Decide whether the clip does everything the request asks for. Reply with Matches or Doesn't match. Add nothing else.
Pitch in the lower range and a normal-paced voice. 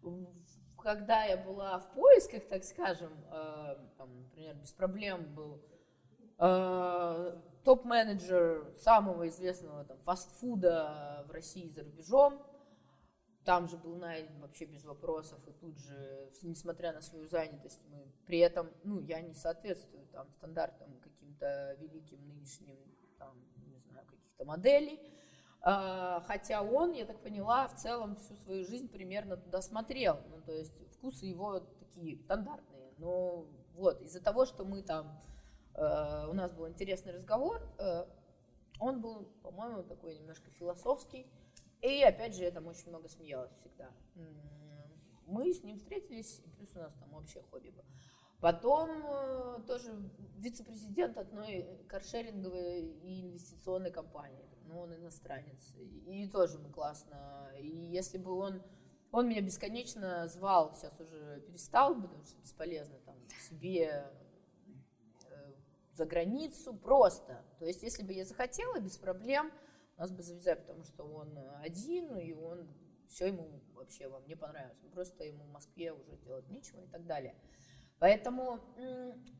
Doesn't match